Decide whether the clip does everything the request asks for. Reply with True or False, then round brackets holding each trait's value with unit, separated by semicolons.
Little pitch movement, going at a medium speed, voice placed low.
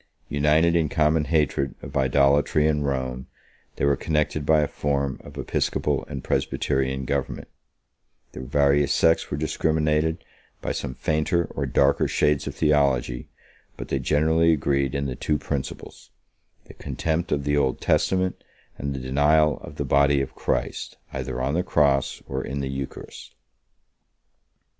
True (2.1 semitones; 150 wpm; 70 Hz)